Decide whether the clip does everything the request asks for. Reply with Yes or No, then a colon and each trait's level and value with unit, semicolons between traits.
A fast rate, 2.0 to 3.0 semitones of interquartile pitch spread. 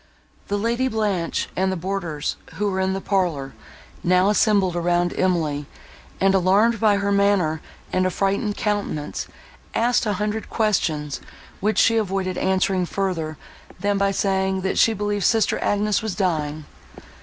No: average, 145 wpm; average, 2.7 semitones